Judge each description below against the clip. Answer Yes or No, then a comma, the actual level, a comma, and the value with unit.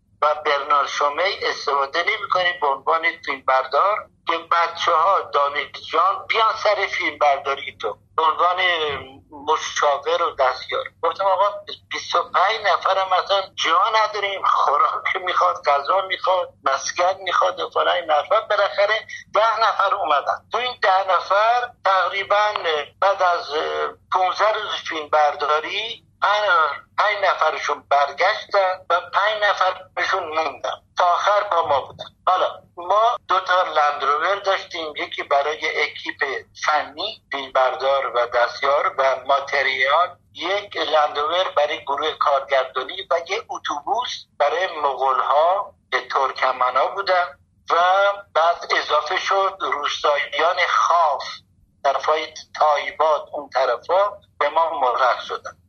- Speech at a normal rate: Yes, average, 120 wpm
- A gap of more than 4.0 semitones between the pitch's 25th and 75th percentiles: Yes, average, 5.2 semitones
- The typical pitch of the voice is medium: Yes, medium, 170 Hz